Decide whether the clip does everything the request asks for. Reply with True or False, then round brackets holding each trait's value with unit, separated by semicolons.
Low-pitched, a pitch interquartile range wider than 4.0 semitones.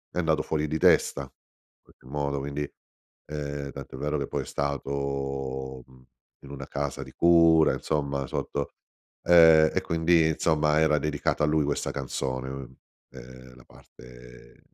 False (70 Hz; 2.4 semitones)